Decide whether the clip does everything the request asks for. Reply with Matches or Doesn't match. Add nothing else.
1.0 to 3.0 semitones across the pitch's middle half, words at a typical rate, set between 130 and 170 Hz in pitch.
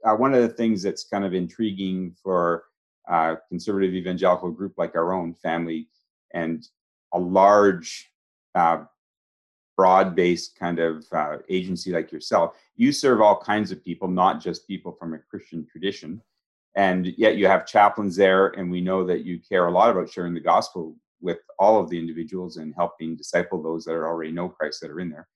Doesn't match